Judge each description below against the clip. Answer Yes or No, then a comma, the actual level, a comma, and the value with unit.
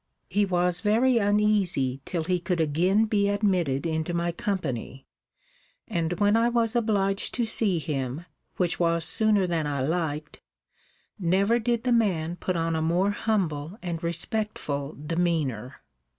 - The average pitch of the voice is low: No, medium, 175 Hz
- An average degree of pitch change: Yes, average, 4.5 semitones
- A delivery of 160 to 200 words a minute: No, average, 145 wpm